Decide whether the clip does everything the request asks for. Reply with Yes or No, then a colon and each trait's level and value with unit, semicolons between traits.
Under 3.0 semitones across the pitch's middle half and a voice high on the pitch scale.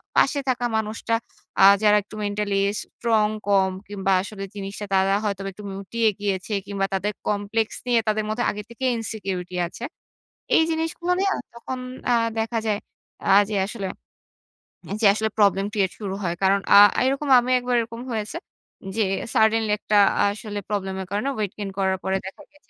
Yes: narrow, 2.5 semitones; high, 210 Hz